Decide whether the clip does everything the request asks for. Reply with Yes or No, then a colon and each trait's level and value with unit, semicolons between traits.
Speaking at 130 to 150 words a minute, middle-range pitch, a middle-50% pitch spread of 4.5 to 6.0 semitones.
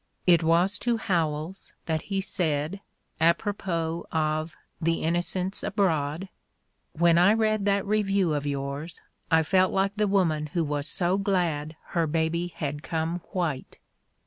No: average, 140 wpm; medium, 170 Hz; average, 3.7 semitones